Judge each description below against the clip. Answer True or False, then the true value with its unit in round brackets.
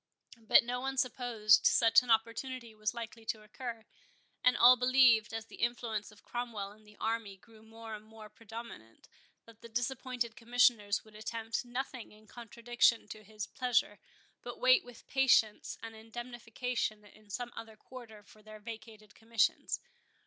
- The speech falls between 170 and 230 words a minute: False (155 wpm)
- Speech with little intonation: True (2.1 semitones)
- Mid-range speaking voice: False (225 Hz)